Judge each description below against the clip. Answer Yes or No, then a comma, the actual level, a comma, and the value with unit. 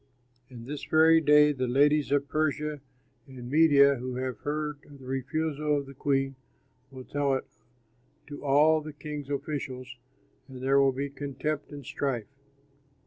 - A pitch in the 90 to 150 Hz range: Yes, medium, 140 Hz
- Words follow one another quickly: No, average, 155 wpm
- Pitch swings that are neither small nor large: No, narrow, 1.9 semitones